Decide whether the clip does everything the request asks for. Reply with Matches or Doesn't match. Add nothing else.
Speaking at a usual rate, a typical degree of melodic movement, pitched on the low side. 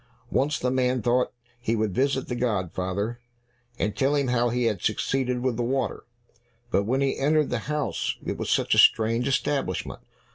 Matches